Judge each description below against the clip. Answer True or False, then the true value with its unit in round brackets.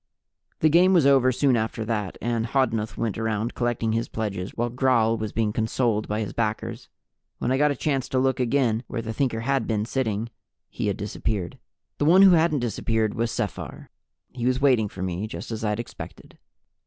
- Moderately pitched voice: False (115 Hz)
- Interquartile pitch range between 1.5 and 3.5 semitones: True (3.1 semitones)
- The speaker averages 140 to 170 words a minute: False (195 wpm)